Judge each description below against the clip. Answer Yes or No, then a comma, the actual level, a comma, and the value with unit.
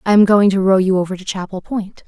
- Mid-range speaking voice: No, high, 195 Hz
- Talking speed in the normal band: No, fast, 290 wpm